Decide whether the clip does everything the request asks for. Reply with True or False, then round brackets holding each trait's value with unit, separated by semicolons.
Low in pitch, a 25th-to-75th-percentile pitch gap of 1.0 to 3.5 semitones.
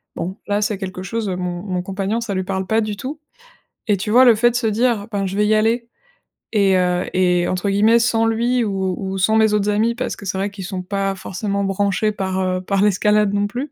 False (200 Hz; 2.6 semitones)